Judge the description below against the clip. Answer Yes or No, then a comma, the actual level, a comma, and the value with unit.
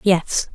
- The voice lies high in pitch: No, medium, 180 Hz